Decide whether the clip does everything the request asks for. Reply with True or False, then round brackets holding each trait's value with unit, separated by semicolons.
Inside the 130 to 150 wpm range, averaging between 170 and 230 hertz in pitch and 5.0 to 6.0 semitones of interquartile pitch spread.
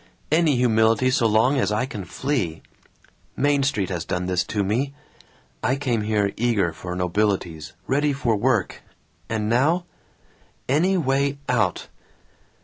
False (140 wpm; 115 Hz; 5.4 semitones)